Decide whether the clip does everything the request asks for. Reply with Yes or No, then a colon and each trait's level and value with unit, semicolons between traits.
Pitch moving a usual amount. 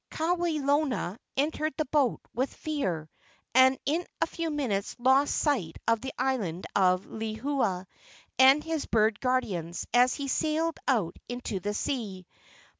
No: wide, 6.0 semitones